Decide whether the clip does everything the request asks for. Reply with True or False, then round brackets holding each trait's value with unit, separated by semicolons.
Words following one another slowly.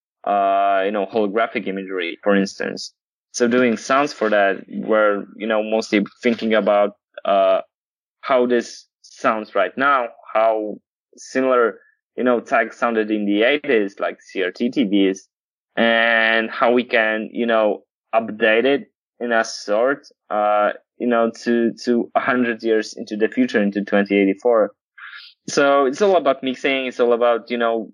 False (155 wpm)